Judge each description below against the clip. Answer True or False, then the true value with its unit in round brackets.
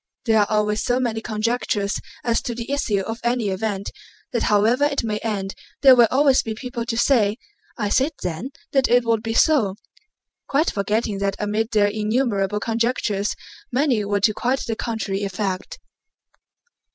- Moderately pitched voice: False (225 Hz)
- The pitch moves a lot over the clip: False (3.0 semitones)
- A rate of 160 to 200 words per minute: True (165 wpm)